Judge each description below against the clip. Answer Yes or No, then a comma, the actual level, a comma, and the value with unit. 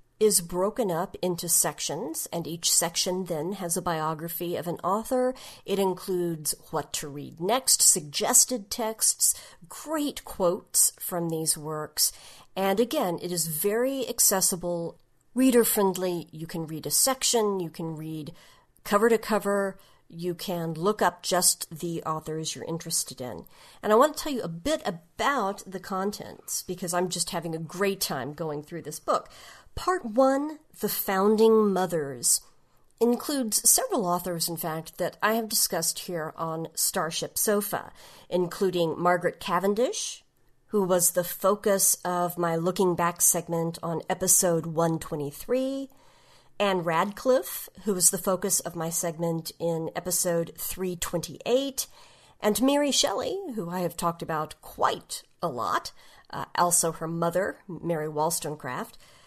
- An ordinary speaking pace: Yes, average, 145 wpm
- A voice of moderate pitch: Yes, medium, 180 Hz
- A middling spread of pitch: Yes, average, 3.7 semitones